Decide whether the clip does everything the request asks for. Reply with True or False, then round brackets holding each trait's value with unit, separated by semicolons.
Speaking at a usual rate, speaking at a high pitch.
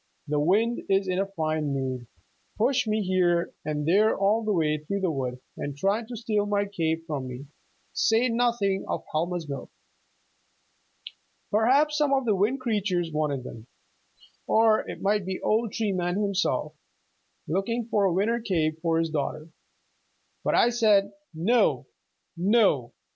True (155 wpm; 195 Hz)